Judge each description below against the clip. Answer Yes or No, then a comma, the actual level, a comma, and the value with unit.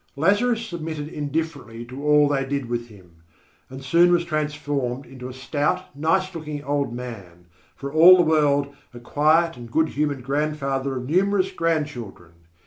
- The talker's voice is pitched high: No, medium, 145 Hz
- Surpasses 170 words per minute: No, average, 155 wpm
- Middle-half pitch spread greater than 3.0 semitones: Yes, average, 3.9 semitones